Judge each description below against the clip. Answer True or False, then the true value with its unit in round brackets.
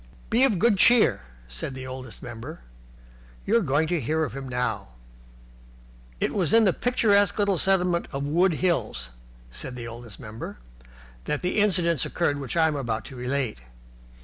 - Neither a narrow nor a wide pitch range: False (7.0 semitones)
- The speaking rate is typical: True (170 wpm)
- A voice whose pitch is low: False (150 Hz)